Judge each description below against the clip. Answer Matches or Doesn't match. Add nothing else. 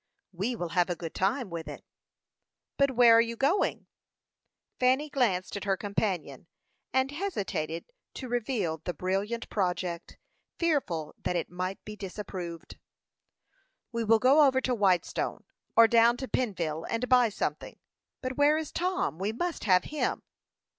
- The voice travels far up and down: Matches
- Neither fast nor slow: Matches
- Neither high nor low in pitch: Doesn't match